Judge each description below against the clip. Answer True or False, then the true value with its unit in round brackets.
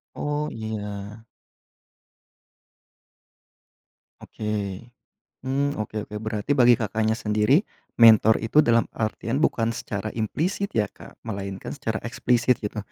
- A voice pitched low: True (110 Hz)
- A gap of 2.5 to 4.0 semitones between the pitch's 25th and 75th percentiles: True (2.9 semitones)